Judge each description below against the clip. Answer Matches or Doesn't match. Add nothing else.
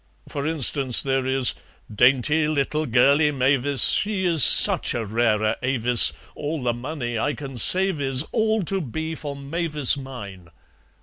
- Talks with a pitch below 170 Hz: Matches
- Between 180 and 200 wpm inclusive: Doesn't match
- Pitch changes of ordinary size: Matches